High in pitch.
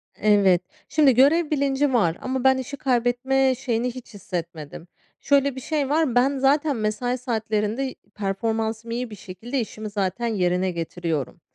Yes: high, 240 Hz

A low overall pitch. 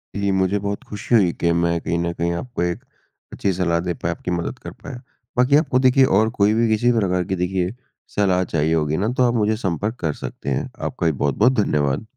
Yes: very low, 95 Hz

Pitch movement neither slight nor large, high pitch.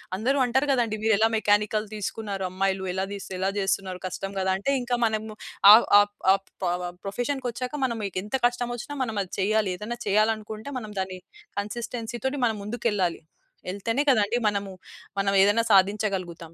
Yes: average, 3.3 semitones; high, 210 Hz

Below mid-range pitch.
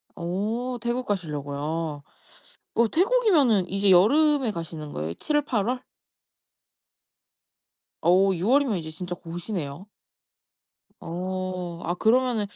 No: high, 190 Hz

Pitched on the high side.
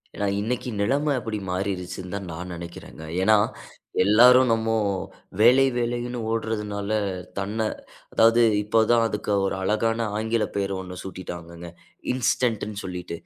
No: low, 105 Hz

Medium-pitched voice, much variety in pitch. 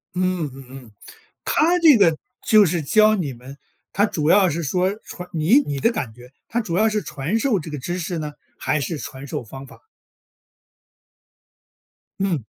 Yes: medium, 170 Hz; wide, 6.5 semitones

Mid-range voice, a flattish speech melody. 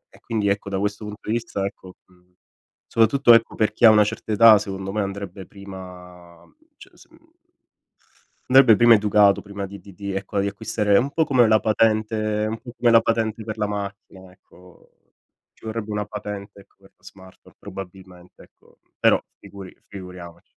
No: low, 105 Hz; narrow, 2.2 semitones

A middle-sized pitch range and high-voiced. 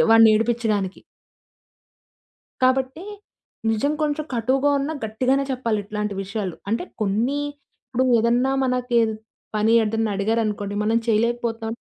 Yes: average, 3.1 semitones; high, 225 Hz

